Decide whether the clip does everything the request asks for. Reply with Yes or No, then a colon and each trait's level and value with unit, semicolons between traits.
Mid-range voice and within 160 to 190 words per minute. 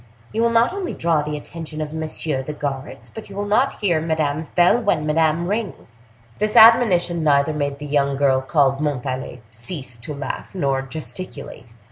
Yes: medium, 155 Hz; average, 175 wpm